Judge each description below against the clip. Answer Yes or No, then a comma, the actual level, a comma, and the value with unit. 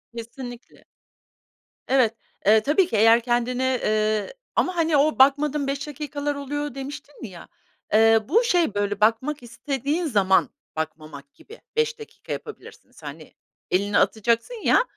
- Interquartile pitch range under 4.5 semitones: No, average, 5.2 semitones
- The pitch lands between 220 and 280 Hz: Yes, very high, 260 Hz